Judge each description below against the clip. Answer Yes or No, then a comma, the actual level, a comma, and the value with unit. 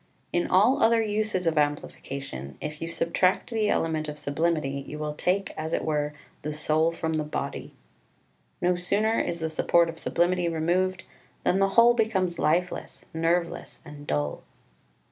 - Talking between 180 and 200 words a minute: No, average, 160 wpm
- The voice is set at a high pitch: No, medium, 165 Hz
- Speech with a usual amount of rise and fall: Yes, average, 3.4 semitones